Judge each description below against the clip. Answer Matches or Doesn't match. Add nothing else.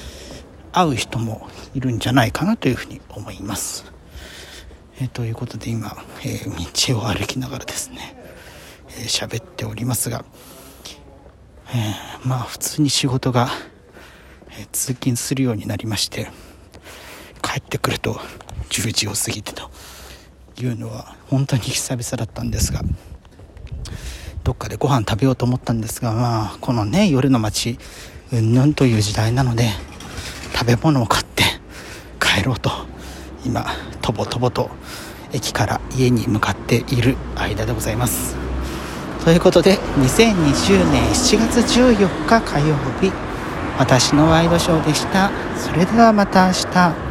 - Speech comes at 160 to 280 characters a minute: Matches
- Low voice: Matches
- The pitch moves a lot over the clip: Matches